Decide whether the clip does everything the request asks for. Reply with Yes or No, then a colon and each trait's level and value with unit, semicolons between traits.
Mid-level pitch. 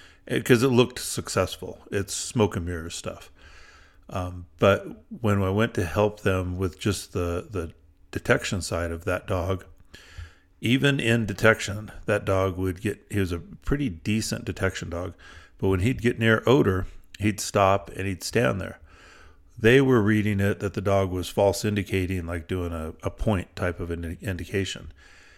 No: very low, 95 Hz